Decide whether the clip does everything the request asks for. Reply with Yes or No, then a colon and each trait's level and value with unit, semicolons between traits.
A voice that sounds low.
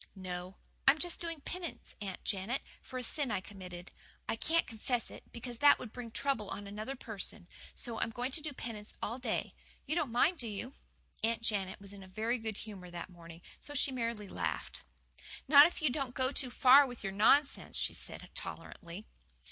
No: high, 230 Hz